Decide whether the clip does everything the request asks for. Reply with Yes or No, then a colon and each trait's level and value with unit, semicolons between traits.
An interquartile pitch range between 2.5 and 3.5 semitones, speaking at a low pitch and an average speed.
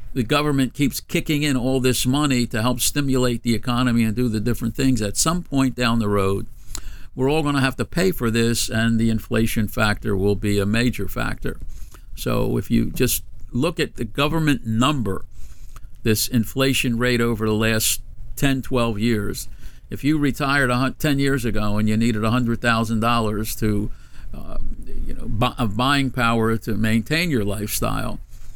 Yes: average, 3.0 semitones; low, 120 Hz; average, 175 wpm